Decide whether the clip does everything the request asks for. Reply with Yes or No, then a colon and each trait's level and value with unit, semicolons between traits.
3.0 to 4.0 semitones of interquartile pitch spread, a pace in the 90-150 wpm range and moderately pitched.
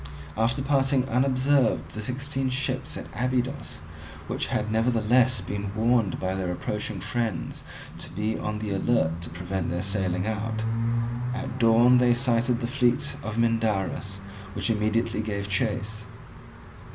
No: average, 3.4 semitones; average, 140 wpm; low, 115 Hz